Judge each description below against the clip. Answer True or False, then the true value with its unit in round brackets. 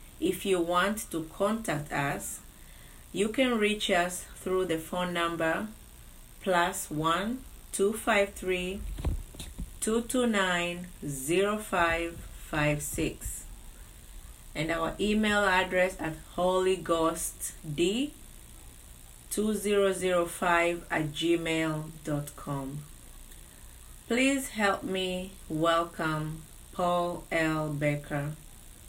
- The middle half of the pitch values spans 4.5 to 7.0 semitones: False (3.7 semitones)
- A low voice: False (175 Hz)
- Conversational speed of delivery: False (60 wpm)